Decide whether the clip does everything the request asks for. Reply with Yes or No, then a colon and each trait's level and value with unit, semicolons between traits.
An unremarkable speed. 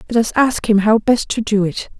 No: fast, 270 wpm